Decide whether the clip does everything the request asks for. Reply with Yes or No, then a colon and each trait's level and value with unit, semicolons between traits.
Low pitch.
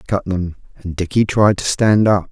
Yes: low, 100 Hz